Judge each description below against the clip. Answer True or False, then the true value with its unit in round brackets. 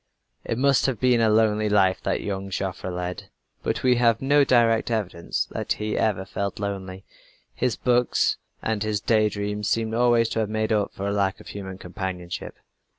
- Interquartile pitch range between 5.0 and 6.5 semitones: False (2.9 semitones)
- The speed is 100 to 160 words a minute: False (185 wpm)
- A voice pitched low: True (105 Hz)